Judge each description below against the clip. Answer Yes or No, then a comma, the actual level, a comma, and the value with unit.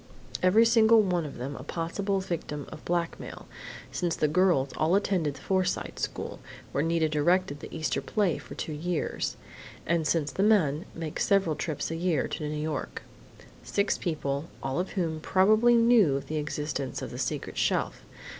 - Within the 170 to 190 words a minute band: Yes, average, 175 wpm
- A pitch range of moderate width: Yes, average, 4.0 semitones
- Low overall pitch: No, medium, 165 Hz